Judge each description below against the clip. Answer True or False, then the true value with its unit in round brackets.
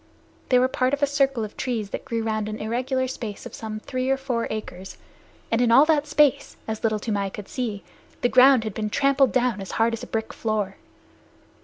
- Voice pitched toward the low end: False (230 Hz)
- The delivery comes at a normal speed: False (215 wpm)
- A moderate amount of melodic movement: True (3.4 semitones)